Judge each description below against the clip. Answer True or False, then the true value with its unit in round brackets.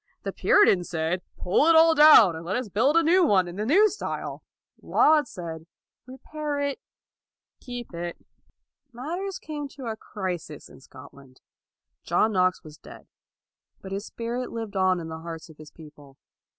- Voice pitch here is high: True (205 Hz)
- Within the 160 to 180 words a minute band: True (175 wpm)